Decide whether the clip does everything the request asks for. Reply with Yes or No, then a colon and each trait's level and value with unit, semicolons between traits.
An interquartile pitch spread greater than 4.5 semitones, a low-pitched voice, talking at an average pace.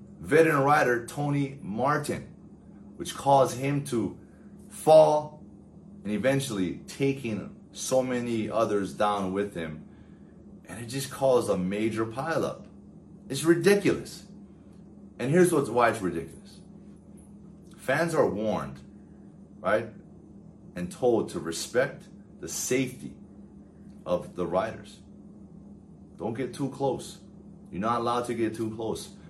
No: average, 5.1 semitones; low, 125 Hz; slow, 115 wpm